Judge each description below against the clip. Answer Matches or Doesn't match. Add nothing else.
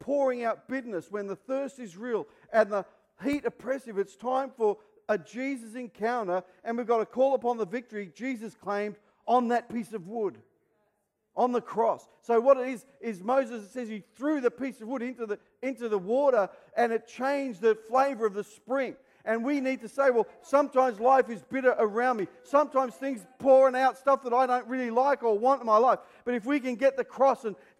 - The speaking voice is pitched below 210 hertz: Doesn't match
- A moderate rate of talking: Doesn't match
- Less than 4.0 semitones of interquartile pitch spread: Matches